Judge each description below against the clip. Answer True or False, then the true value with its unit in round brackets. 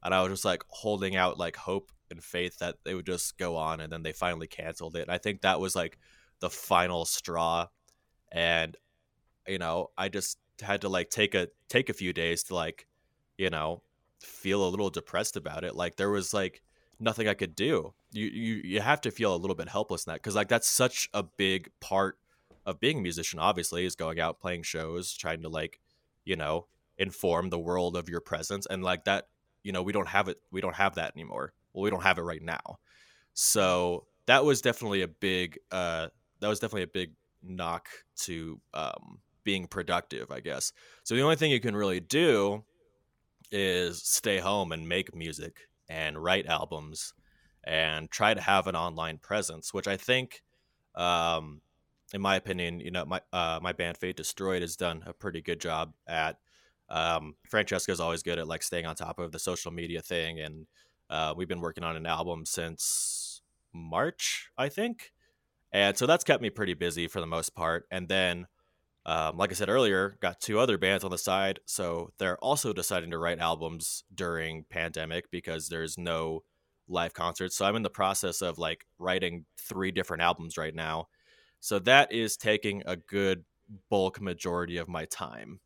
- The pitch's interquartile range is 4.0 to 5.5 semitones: False (2.7 semitones)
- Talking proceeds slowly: False (195 wpm)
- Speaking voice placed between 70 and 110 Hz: True (90 Hz)